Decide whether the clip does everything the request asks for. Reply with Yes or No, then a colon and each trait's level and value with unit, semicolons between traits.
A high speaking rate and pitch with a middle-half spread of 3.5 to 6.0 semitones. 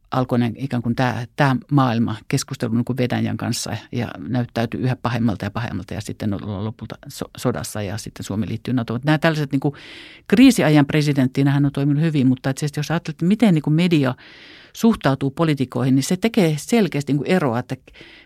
Yes: fast, 175 wpm; average, 4.2 semitones